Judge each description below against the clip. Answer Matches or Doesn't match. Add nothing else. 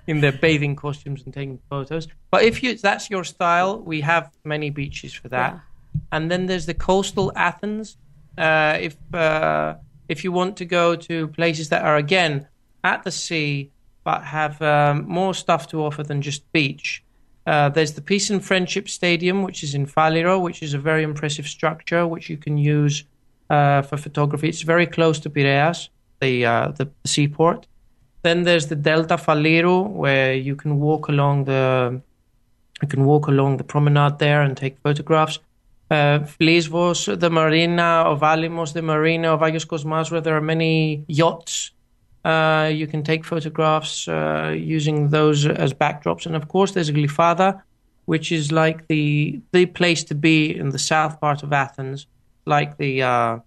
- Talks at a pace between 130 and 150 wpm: Doesn't match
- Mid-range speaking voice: Matches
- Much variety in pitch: Doesn't match